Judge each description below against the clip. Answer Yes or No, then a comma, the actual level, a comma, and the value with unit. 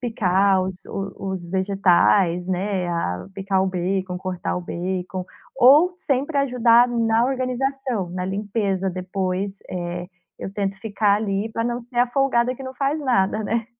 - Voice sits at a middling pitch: No, high, 200 Hz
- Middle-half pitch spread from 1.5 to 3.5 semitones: No, average, 4.5 semitones